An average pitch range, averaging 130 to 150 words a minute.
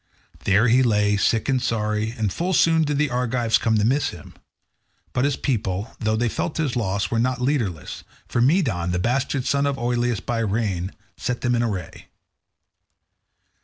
No: average, 3.8 semitones; average, 175 wpm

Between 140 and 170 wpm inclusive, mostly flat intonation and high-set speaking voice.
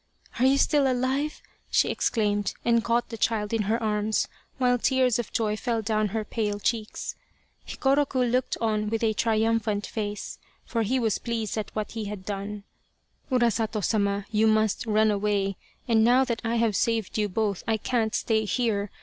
No: average, 185 wpm; narrow, 2.1 semitones; high, 220 Hz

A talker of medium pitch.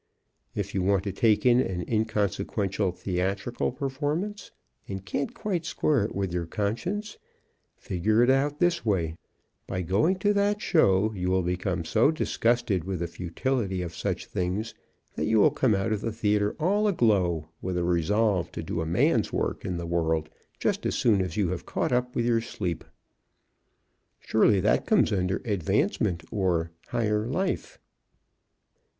No: low, 105 Hz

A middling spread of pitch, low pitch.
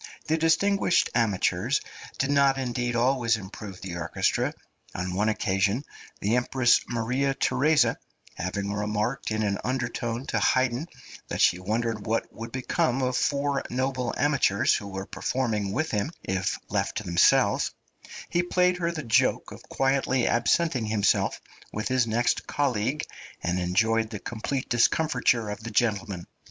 Yes: average, 4.2 semitones; low, 120 Hz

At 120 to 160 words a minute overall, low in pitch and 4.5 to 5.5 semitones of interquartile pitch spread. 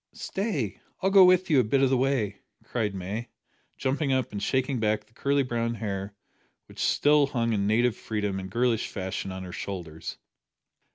No: average, 180 wpm; low, 115 Hz; average, 5.1 semitones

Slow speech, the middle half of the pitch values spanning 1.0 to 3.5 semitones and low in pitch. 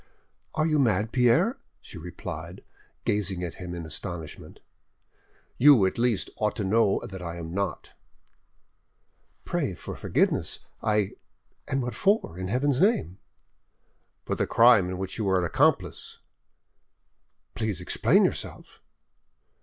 No: slow, 130 wpm; wide, 5.4 semitones; low, 100 Hz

